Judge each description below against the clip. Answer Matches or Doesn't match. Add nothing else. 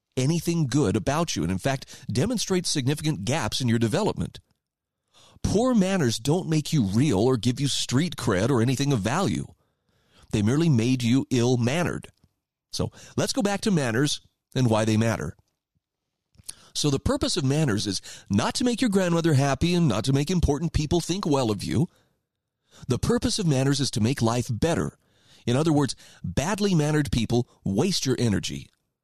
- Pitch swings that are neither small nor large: Doesn't match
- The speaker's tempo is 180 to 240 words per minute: Doesn't match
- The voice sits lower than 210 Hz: Matches